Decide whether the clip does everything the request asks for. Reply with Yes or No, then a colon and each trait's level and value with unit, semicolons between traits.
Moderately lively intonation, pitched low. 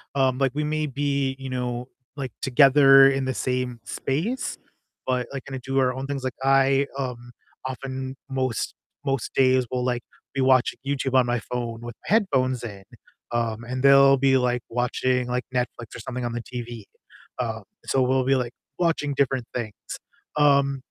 No: narrow, 1.7 semitones; low, 130 Hz